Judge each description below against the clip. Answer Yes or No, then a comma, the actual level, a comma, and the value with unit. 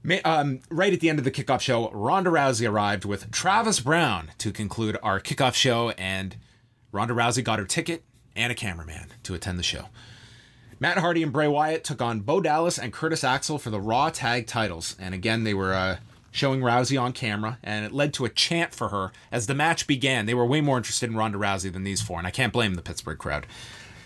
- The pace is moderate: No, fast, 220 wpm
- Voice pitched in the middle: No, low, 120 Hz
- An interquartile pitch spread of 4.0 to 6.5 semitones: Yes, average, 4.8 semitones